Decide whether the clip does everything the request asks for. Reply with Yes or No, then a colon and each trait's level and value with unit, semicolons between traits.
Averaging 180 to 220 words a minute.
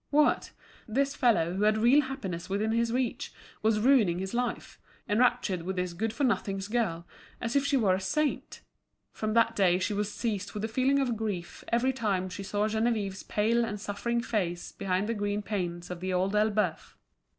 Yes: average, 190 wpm